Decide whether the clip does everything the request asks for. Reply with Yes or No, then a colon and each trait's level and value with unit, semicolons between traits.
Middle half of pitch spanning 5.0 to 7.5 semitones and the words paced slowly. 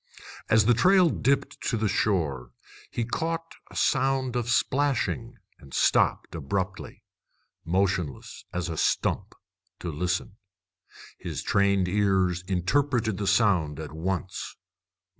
Yes: average, 5.3 semitones; slow, 120 wpm